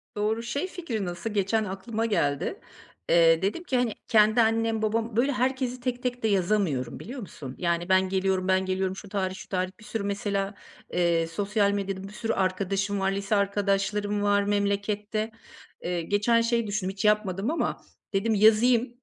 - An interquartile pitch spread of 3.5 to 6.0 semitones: No, average, 2.8 semitones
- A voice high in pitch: Yes, high, 205 Hz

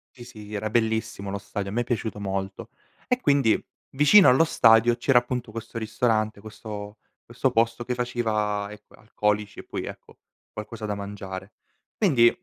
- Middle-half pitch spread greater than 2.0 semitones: Yes, narrow, 2.6 semitones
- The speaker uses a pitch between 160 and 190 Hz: No, low, 110 Hz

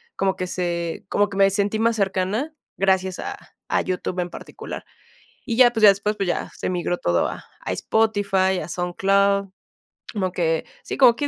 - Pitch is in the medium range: No, high, 195 Hz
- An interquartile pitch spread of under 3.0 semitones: Yes, narrow, 2.4 semitones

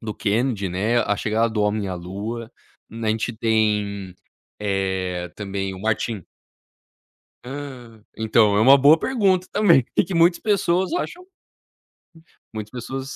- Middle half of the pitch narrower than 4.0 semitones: No, average, 4.9 semitones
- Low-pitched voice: Yes, low, 110 Hz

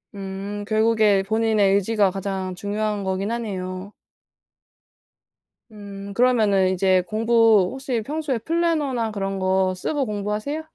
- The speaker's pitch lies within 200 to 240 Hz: Yes, high, 205 Hz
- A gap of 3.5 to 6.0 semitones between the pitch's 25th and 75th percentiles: No, average, 2.8 semitones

